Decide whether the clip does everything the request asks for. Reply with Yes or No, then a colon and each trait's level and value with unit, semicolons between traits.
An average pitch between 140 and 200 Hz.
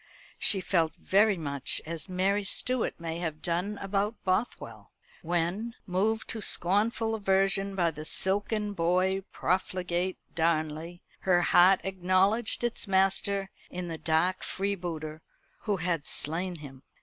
Yes: medium, 185 Hz